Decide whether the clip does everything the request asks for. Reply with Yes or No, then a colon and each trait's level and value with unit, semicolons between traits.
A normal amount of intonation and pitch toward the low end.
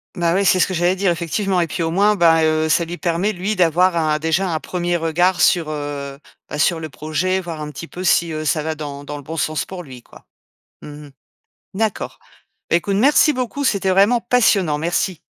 No: average, 3.2 semitones; medium, 170 Hz